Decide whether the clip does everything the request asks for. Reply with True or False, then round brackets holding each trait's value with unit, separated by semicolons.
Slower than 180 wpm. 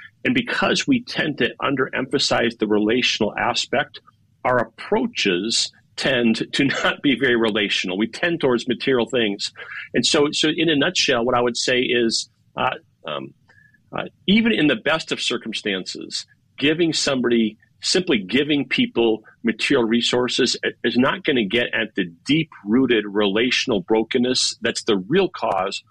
True (145 wpm)